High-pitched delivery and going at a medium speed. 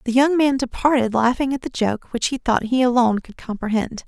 No: high, 245 Hz; fast, 220 wpm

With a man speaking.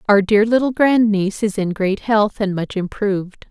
No: female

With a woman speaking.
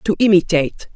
Yes: female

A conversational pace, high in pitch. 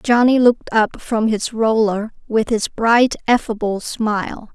Yes: average, 145 wpm; high, 225 Hz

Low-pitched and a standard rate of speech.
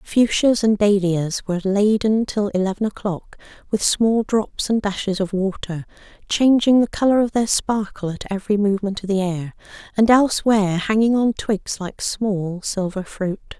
No: high, 205 Hz; average, 160 wpm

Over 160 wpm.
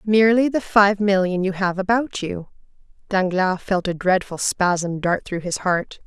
Yes: average, 170 wpm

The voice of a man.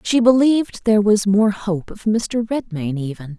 No: female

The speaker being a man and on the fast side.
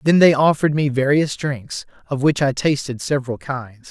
No: male; average, 185 wpm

